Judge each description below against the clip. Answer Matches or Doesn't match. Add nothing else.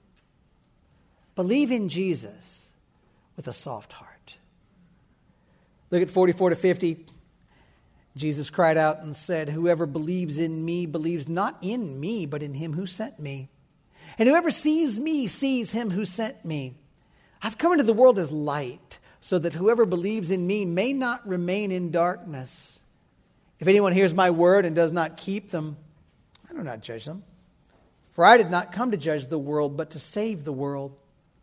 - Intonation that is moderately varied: Matches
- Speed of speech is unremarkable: Matches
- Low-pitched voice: Doesn't match